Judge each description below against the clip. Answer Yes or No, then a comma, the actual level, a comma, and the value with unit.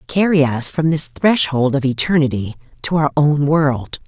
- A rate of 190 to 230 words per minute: No, average, 160 wpm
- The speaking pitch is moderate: Yes, medium, 145 Hz